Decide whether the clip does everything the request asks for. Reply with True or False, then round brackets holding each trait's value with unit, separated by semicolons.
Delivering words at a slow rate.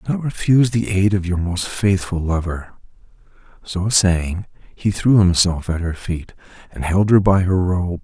False (180 wpm)